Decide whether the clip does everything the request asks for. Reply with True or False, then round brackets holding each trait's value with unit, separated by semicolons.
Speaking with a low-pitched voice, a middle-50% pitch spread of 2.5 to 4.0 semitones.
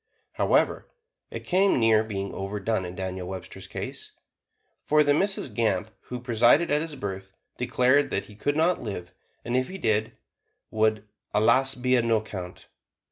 False (115 Hz; 4.8 semitones)